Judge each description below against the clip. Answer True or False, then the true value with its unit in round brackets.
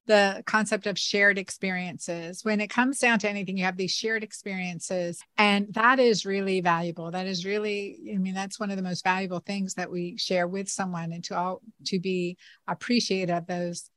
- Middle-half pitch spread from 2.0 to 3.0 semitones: True (2.7 semitones)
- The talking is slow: False (200 wpm)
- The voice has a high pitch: True (195 Hz)